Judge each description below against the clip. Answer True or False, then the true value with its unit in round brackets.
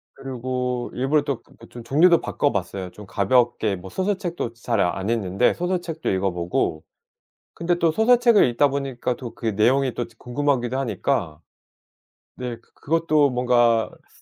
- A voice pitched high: False (125 Hz)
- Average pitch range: True (4.7 semitones)